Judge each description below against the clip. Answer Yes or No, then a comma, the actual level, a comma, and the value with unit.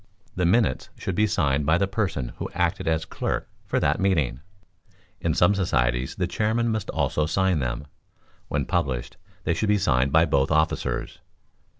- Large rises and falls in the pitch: Yes, wide, 6.3 semitones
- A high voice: No, very low, 80 Hz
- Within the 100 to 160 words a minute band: No, average, 170 wpm